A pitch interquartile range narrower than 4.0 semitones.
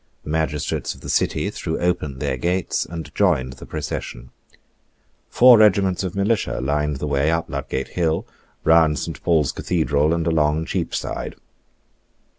Yes: average, 3.4 semitones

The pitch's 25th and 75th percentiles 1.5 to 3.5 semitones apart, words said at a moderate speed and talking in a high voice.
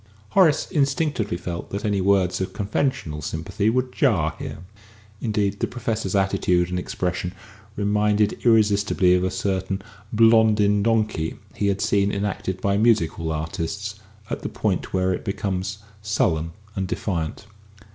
No: average, 2.8 semitones; average, 145 wpm; low, 100 Hz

